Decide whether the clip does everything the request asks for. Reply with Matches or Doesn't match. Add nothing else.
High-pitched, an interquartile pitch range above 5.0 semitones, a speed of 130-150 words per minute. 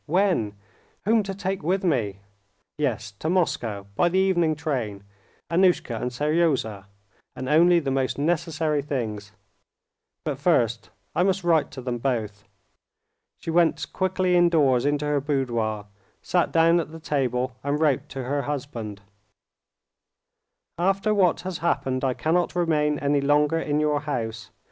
Doesn't match